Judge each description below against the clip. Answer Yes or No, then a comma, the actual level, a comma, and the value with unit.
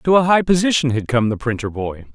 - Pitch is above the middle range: No, low, 135 Hz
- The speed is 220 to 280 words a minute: Yes, fast, 250 wpm